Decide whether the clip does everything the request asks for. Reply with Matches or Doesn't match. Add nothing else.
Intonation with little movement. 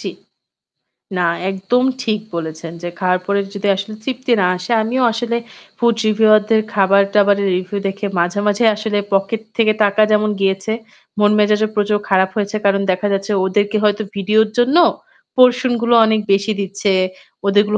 Matches